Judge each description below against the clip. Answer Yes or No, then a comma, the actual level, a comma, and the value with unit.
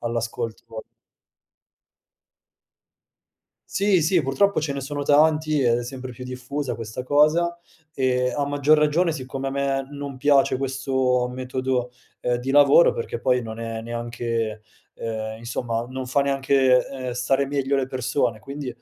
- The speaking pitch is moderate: No, low, 130 Hz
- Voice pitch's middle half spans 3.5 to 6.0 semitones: No, average, 2.7 semitones